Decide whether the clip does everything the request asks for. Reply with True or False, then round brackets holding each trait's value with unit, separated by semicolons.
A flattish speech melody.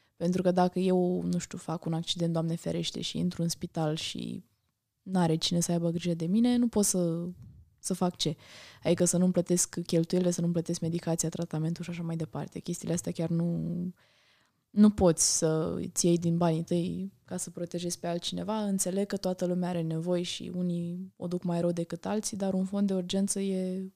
True (1.6 semitones)